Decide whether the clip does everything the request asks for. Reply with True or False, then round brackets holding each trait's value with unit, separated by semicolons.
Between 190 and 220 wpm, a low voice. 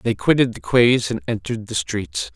True (205 wpm; 115 Hz)